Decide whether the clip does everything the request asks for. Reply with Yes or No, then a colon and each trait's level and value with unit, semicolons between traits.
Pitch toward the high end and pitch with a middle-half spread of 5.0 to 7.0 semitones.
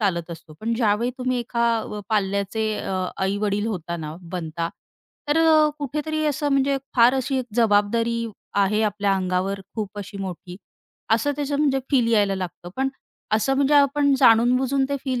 Yes: high, 225 Hz; wide, 5.4 semitones